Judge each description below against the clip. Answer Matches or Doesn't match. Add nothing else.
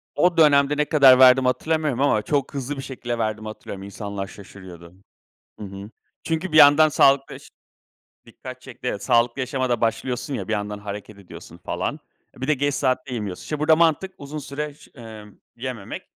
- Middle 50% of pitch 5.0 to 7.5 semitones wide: Matches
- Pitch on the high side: Doesn't match